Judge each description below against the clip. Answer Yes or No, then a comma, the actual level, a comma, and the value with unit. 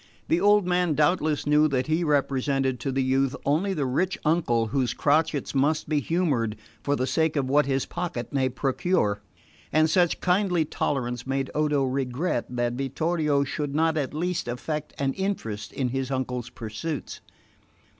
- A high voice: No, medium, 140 Hz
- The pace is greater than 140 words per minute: Yes, average, 165 wpm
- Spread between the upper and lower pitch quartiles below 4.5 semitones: Yes, average, 3.5 semitones